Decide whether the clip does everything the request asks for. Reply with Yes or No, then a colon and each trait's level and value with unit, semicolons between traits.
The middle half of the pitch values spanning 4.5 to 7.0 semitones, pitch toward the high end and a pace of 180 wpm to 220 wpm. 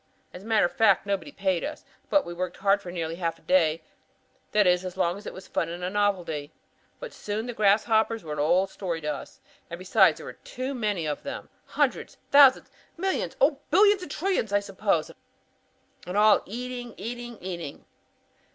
Yes: average, 5.1 semitones; high, 200 Hz; average, 190 wpm